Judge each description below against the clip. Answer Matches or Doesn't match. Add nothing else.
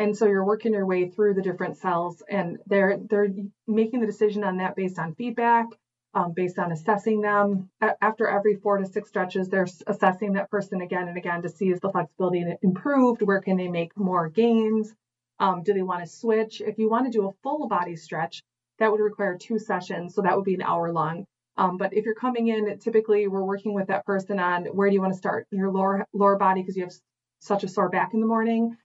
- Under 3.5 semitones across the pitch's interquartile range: Matches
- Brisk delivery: Matches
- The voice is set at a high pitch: Matches